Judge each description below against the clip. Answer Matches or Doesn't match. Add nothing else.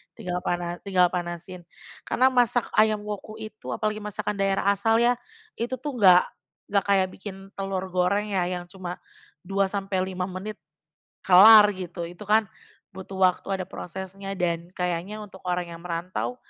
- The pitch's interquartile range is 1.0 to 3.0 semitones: Matches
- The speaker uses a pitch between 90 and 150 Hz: Doesn't match